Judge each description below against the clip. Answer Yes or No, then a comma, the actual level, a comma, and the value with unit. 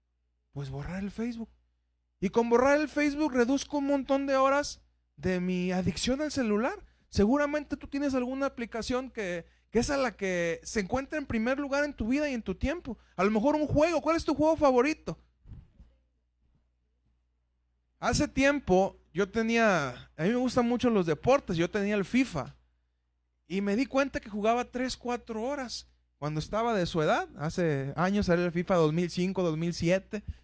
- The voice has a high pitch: Yes, high, 210 Hz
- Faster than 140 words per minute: Yes, average, 175 wpm